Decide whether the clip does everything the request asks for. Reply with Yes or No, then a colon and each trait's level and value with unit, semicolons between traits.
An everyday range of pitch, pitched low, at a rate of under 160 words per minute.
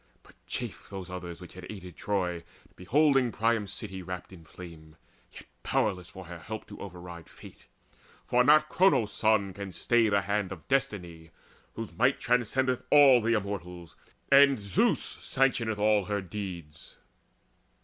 Yes: average, 4.5 semitones; low, 100 Hz; average, 150 wpm